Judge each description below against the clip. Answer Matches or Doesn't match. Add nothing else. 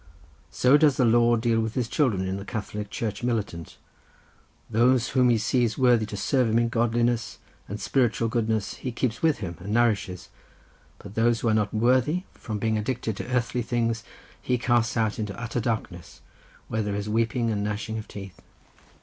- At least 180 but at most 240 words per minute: Matches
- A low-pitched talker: Matches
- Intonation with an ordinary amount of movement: Doesn't match